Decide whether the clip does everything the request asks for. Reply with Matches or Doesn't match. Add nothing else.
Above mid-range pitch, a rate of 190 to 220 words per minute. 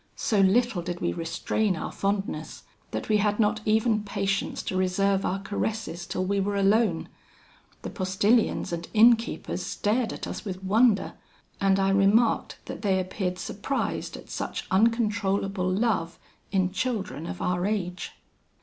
Doesn't match